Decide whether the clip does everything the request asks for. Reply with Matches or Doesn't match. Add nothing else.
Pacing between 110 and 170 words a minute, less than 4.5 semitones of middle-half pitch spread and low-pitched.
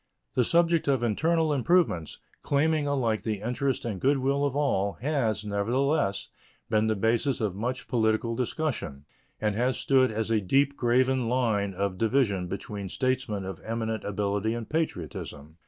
Doesn't match